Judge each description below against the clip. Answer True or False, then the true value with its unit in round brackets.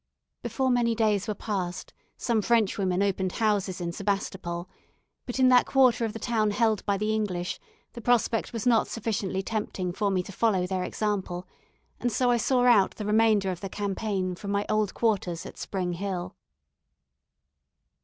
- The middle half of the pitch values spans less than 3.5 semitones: True (3.1 semitones)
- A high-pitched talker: True (205 Hz)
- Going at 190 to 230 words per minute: False (170 wpm)